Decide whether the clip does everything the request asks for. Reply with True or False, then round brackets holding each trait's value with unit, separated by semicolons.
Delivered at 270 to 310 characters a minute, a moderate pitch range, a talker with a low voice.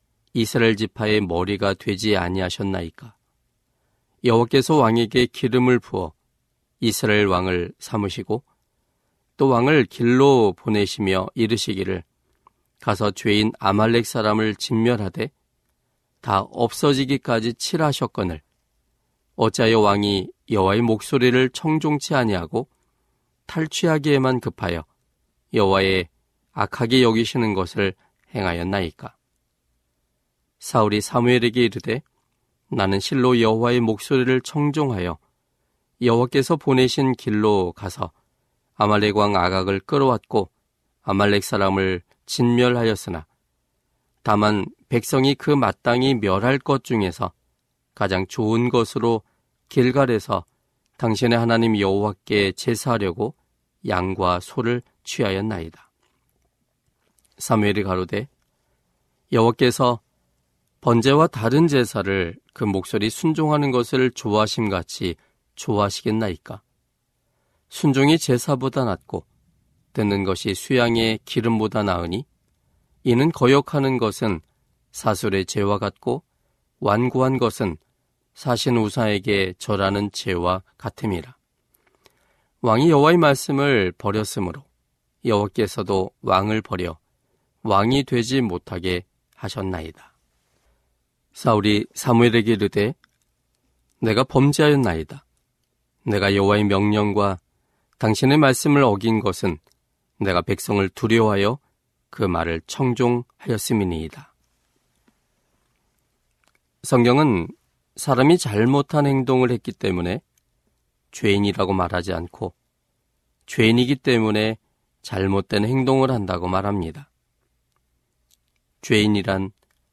False (245 characters per minute; 4.5 semitones; 110 Hz)